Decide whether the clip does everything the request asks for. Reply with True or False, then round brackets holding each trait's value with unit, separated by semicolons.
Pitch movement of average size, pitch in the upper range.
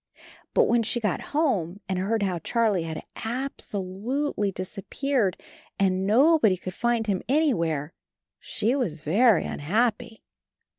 True (4.6 semitones; 210 Hz)